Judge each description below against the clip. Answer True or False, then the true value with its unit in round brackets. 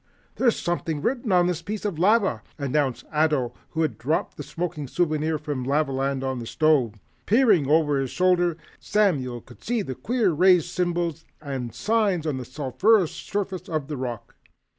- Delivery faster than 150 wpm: True (160 wpm)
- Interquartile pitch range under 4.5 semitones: False (5.1 semitones)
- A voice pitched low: False (155 Hz)